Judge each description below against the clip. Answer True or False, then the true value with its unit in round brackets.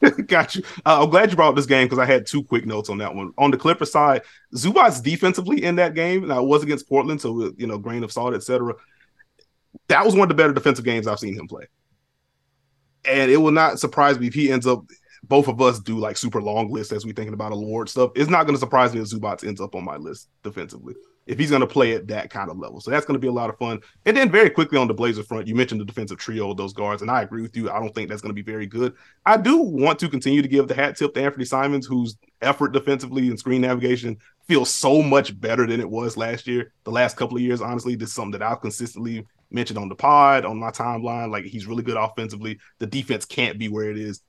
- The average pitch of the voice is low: True (120 Hz)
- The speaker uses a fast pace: True (265 wpm)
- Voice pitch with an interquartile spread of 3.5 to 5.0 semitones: True (3.8 semitones)